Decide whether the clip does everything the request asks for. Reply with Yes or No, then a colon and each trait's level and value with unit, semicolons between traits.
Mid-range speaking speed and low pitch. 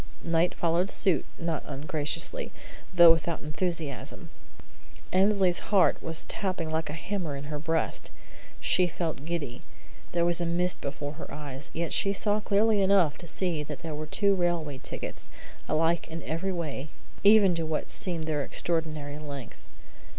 No: average, 160 wpm; medium, 165 Hz